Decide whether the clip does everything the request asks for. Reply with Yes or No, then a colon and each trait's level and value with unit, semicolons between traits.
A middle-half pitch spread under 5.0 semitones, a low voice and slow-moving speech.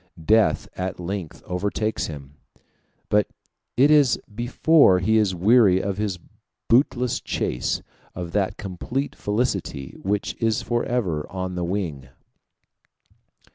Yes: average, 4.3 semitones; low, 100 Hz; slow, 115 wpm